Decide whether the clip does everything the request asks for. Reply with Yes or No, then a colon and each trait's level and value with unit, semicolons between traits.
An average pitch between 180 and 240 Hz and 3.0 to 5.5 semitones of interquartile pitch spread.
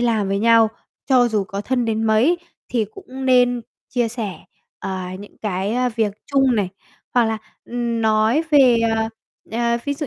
No: high, 230 Hz; narrow, 2.5 semitones